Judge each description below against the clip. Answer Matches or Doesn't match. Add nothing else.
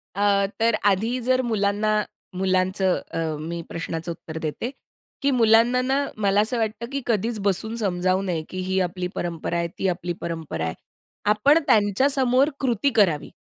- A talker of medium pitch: Doesn't match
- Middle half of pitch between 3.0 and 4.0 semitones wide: Doesn't match